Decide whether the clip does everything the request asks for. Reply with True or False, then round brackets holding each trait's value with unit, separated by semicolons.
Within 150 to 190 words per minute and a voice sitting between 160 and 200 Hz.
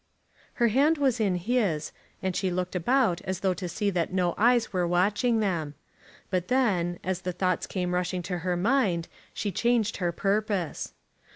True (175 wpm; 185 Hz)